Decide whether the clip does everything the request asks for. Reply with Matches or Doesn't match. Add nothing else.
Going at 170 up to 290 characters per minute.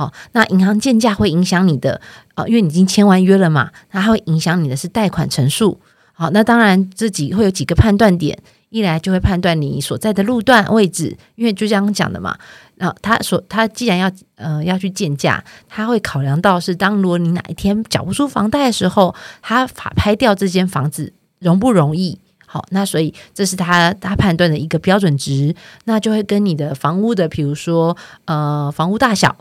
Doesn't match